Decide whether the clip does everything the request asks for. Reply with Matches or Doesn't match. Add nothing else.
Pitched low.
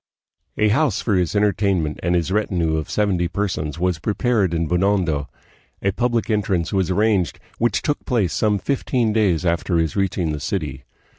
Matches